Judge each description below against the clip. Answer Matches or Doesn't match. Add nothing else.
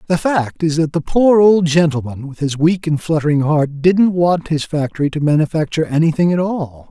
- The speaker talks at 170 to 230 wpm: Matches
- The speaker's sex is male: Matches